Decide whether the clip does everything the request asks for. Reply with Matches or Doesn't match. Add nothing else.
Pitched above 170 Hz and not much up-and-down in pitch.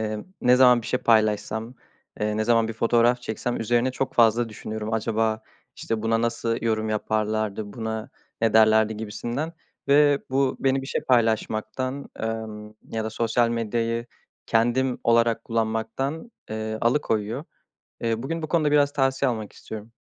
Doesn't match